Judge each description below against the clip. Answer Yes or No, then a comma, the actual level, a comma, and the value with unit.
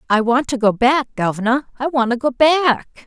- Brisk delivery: No, average, 195 wpm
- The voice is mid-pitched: No, very high, 255 Hz